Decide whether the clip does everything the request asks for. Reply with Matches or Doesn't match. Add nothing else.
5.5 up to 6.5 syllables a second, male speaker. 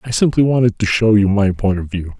Matches